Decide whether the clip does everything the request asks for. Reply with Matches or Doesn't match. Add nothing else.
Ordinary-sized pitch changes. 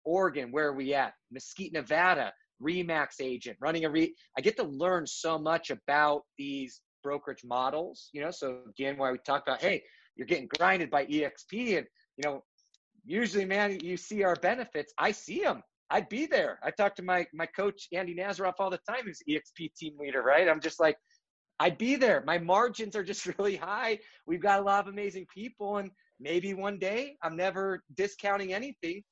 Matches